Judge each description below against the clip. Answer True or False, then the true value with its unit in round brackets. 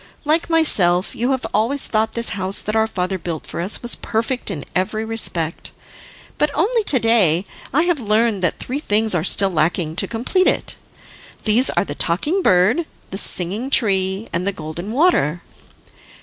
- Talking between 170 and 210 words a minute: True (175 wpm)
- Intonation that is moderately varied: False (5.7 semitones)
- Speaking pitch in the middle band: False (215 Hz)